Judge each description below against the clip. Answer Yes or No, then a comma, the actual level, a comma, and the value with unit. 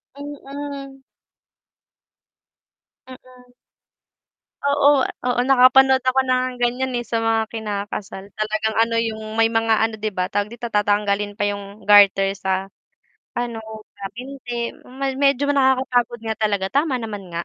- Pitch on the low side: No, high, 230 Hz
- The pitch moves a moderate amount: Yes, average, 3.7 semitones